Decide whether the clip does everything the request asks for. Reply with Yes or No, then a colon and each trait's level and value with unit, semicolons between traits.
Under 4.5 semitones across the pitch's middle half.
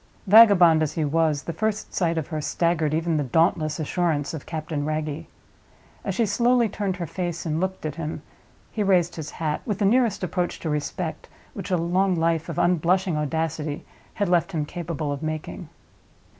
Yes: average, 3.0 semitones